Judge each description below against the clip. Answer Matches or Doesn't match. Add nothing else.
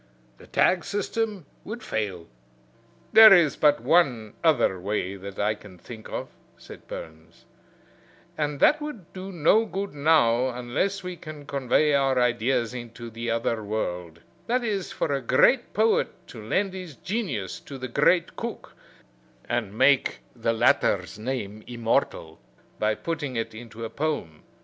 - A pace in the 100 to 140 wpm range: Doesn't match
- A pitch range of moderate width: Doesn't match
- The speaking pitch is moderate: Doesn't match